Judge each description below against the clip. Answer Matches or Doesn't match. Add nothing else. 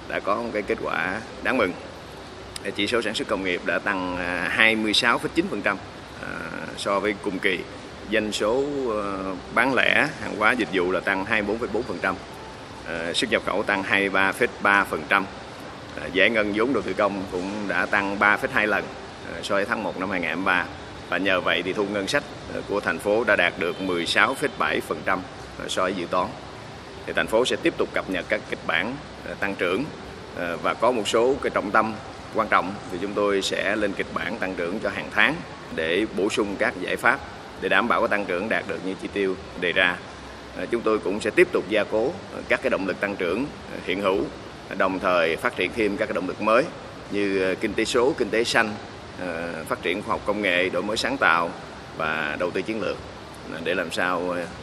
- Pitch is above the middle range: Doesn't match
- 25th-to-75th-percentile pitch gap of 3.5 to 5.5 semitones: Doesn't match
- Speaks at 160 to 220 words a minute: Matches